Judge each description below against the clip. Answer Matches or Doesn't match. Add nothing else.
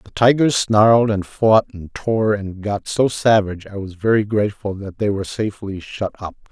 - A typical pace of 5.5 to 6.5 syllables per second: Doesn't match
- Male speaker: Matches